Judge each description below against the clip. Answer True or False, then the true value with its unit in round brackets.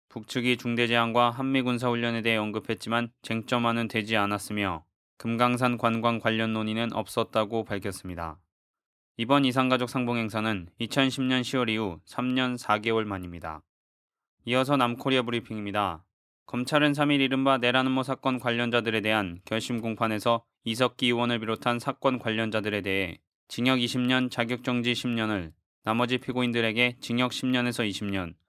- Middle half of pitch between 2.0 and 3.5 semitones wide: True (2.4 semitones)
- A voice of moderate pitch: False (115 Hz)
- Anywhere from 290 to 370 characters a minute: True (325 characters per minute)